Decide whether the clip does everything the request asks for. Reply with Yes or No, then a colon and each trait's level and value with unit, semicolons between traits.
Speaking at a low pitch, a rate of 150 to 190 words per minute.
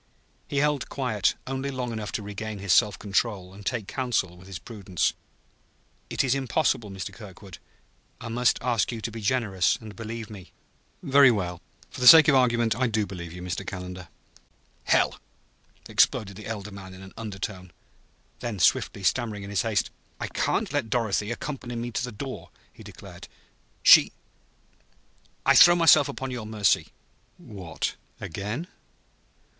Yes: low, 110 Hz; average, 165 wpm